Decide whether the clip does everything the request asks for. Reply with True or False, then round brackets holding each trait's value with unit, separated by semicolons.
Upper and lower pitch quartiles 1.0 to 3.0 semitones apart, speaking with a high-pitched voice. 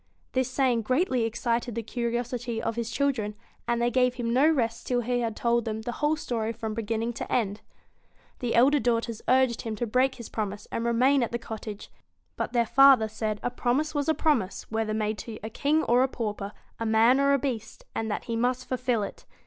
True (2.4 semitones; 235 Hz)